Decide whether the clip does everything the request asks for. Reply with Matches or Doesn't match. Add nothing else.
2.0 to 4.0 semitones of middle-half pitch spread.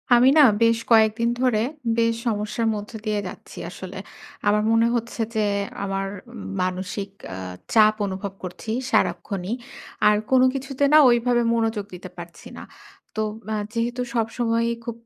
Matches